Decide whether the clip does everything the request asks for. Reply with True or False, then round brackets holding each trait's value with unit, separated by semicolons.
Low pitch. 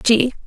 False (235 Hz)